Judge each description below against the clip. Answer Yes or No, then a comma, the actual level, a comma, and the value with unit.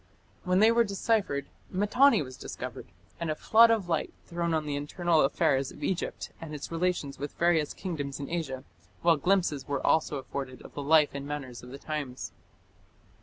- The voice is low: No, medium, 155 Hz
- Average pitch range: Yes, average, 4.1 semitones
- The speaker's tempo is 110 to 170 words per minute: No, average, 180 wpm